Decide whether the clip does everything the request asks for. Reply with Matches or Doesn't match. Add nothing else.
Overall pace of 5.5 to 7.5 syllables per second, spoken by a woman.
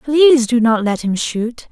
Doesn't match